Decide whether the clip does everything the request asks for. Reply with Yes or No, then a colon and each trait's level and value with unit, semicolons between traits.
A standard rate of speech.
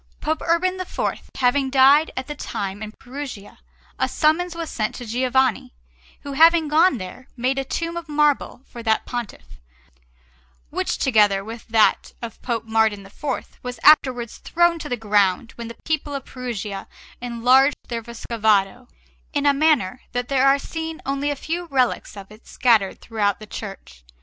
Yes: average, 165 wpm